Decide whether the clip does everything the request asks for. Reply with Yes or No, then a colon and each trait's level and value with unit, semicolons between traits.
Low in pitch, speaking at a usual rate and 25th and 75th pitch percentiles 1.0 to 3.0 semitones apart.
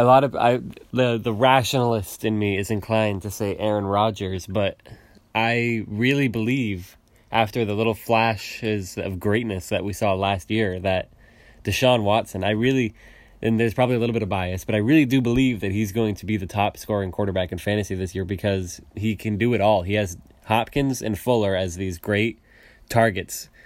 Yes: low, 110 Hz; average, 195 wpm; average, 2.7 semitones